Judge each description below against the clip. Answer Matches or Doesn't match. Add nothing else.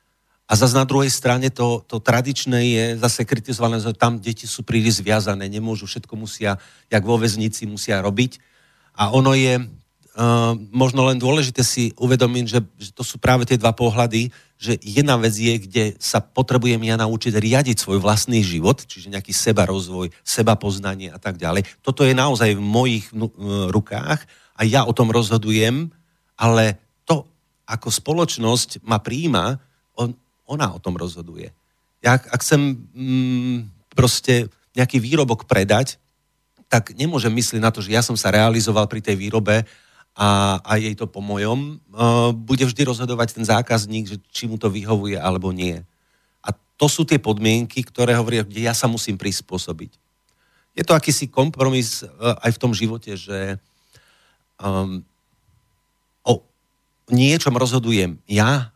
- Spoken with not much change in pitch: Doesn't match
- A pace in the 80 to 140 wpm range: Doesn't match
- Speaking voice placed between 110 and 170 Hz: Matches